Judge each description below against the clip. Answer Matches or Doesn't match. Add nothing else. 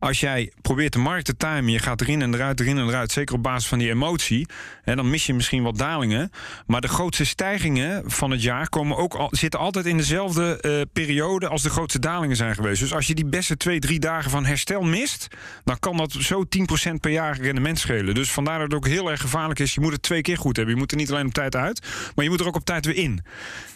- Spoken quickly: Matches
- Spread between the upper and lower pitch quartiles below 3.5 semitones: Doesn't match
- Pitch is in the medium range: Matches